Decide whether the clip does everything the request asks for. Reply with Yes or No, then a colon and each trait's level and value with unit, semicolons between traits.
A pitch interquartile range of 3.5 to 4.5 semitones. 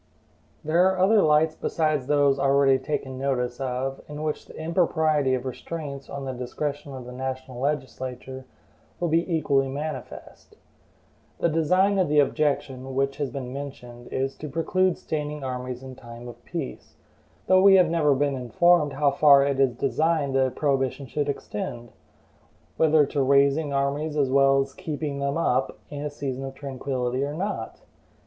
No: narrow, 2.6 semitones